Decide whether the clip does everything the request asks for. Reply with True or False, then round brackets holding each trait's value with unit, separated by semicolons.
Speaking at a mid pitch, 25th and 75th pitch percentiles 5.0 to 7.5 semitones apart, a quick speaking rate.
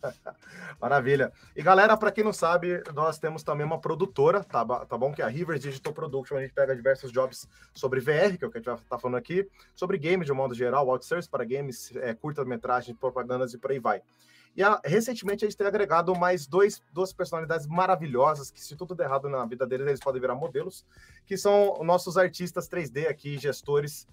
True (155 Hz; 5.4 semitones; 210 wpm)